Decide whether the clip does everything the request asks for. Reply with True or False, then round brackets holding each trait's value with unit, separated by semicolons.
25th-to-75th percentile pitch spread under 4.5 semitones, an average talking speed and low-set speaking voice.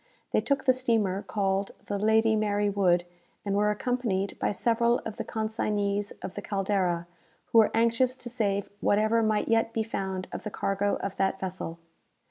False (2.5 semitones; 175 wpm; 210 Hz)